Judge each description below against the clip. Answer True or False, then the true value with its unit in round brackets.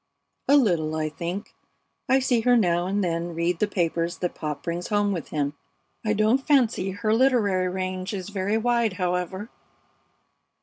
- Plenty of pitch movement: False (4.1 semitones)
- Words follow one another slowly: False (165 wpm)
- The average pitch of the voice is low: False (190 Hz)